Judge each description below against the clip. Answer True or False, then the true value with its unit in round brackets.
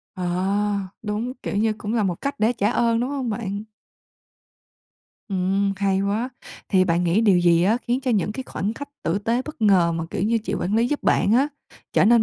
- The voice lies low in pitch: False (210 Hz)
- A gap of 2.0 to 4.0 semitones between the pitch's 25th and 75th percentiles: True (3.6 semitones)